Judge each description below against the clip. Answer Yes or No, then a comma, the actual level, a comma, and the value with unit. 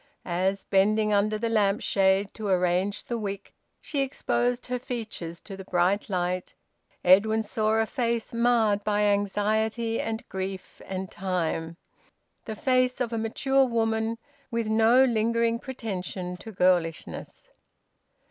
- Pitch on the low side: No, high, 215 Hz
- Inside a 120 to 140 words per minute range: Yes, slow, 135 wpm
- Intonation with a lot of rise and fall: No, average, 3.3 semitones